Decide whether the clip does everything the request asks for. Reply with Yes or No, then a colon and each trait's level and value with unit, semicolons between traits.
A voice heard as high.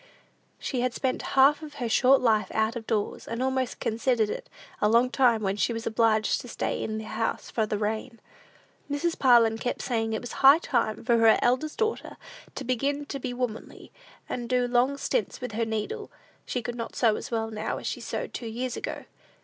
Yes: high, 240 Hz